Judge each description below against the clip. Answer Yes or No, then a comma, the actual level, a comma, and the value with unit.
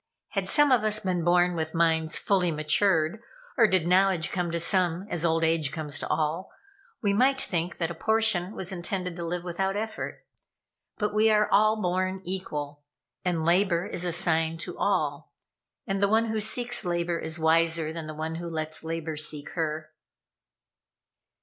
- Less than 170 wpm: No, average, 175 wpm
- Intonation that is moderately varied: Yes, average, 3.2 semitones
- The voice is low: No, medium, 175 Hz